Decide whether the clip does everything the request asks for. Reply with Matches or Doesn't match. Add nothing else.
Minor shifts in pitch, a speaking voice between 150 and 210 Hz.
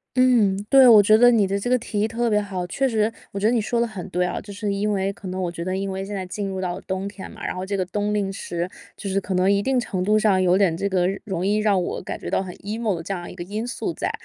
Matches